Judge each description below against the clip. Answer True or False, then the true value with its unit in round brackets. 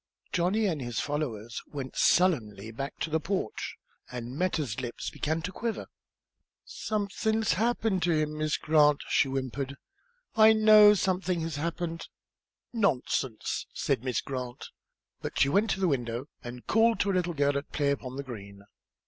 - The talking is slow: False (155 wpm)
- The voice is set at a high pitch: False (155 Hz)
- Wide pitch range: True (6.4 semitones)